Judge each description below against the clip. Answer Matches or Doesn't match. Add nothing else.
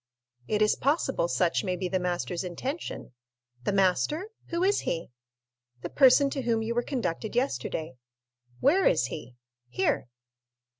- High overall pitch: Matches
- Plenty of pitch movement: Matches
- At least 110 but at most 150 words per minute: Matches